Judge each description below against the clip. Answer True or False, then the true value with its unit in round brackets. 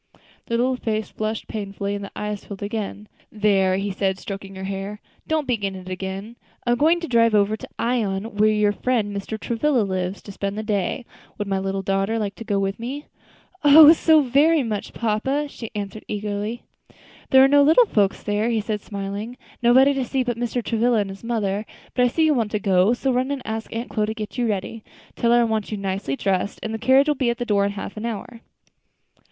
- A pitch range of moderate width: True (3.4 semitones)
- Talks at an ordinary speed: False (225 wpm)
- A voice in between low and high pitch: False (215 Hz)